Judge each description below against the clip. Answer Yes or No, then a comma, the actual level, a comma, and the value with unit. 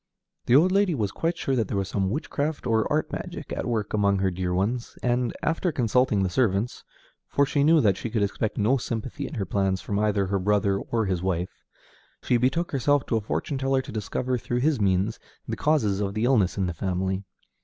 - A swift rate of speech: Yes, fast, 220 wpm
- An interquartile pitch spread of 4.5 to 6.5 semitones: Yes, average, 5.2 semitones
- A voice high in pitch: No, low, 110 Hz